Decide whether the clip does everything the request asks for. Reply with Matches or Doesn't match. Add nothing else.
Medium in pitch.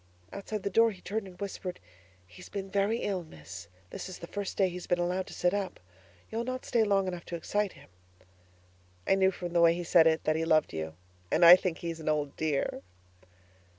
Matches